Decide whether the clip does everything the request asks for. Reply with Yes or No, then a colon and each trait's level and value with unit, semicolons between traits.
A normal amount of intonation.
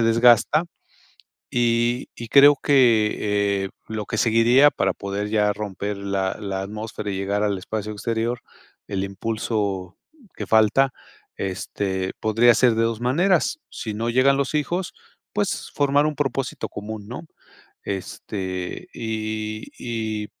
Yes: average, 3.2 semitones